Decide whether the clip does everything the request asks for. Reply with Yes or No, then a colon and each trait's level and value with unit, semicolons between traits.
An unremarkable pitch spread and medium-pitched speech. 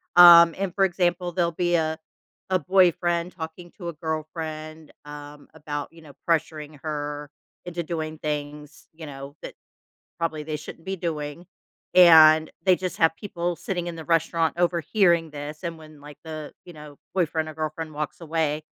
No: narrow, 2.2 semitones; medium, 160 Hz